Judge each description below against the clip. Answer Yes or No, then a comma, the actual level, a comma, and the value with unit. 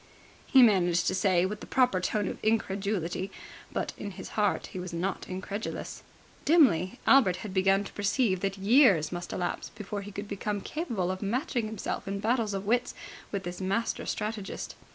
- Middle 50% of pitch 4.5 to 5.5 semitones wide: No, average, 2.7 semitones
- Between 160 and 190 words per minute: Yes, average, 175 wpm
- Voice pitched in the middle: No, high, 200 Hz